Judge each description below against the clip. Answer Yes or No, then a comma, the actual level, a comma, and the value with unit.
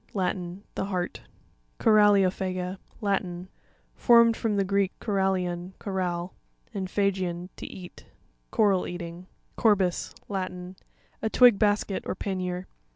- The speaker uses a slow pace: Yes, slow, 120 wpm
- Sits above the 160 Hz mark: Yes, high, 190 Hz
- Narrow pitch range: Yes, narrow, 2.0 semitones